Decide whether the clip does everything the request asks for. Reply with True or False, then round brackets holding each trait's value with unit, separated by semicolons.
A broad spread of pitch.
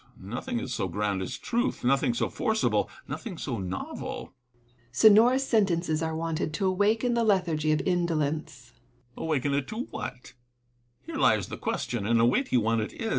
True (8.8 semitones)